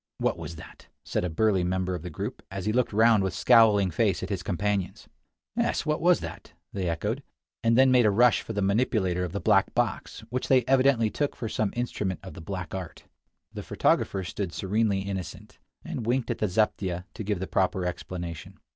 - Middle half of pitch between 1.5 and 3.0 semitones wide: No, average, 3.7 semitones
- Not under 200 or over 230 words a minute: Yes, fast, 205 wpm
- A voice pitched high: No, low, 100 Hz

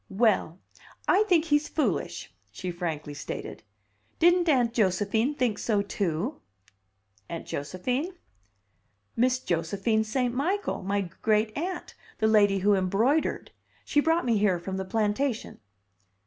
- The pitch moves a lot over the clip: Yes, wide, 6.5 semitones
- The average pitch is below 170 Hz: No, high, 220 Hz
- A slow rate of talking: Yes, slow, 125 wpm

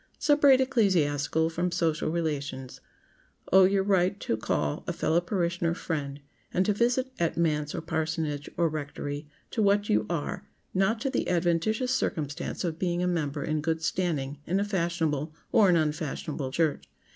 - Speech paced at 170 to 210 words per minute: No, average, 155 wpm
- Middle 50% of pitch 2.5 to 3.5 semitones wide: No, average, 4.2 semitones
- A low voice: No, medium, 165 Hz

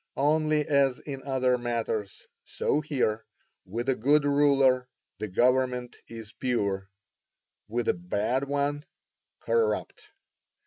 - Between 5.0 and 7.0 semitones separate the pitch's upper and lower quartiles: No, average, 3.8 semitones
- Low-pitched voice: Yes, low, 130 Hz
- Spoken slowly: Yes, slow, 110 wpm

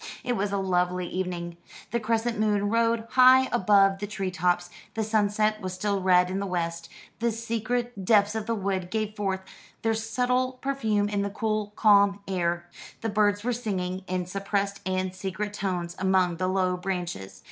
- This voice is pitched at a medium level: No, high, 200 Hz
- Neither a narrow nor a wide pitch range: Yes, average, 3.0 semitones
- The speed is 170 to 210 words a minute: Yes, average, 175 wpm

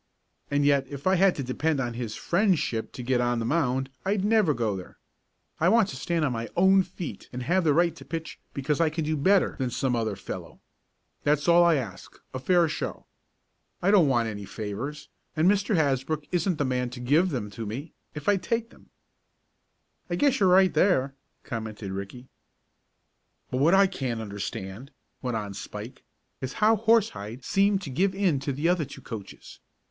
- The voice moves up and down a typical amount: No, wide, 6.6 semitones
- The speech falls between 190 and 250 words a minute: Yes, average, 195 wpm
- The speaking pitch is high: No, medium, 145 Hz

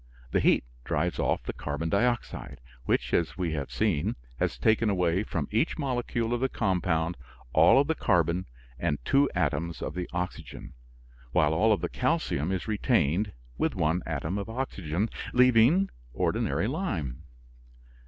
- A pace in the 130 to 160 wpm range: Yes, average, 155 wpm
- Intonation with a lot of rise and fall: Yes, wide, 6.1 semitones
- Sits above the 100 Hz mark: No, very low, 95 Hz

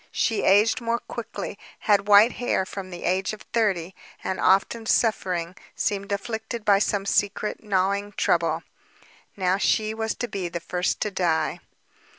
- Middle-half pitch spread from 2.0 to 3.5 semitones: Yes, average, 2.7 semitones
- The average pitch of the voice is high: Yes, high, 200 Hz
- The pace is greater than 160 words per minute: No, average, 155 wpm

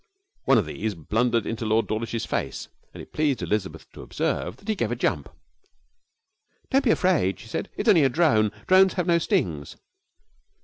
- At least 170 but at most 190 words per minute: Yes, average, 180 wpm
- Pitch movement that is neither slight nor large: No, wide, 8.1 semitones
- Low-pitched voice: Yes, low, 115 Hz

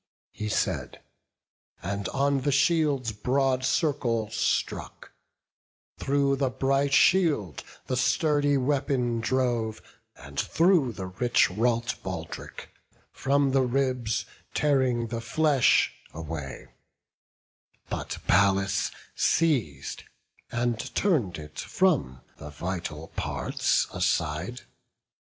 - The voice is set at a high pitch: No, low, 125 Hz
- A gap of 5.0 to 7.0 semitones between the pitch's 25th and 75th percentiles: Yes, wide, 5.6 semitones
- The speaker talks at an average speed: No, slow, 95 wpm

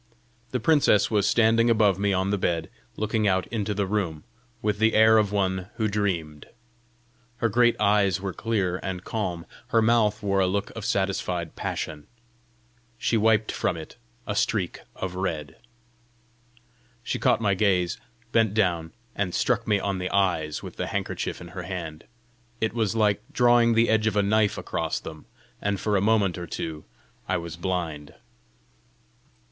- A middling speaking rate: Yes, average, 165 wpm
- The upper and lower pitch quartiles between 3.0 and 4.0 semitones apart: Yes, average, 3.3 semitones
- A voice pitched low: Yes, low, 100 Hz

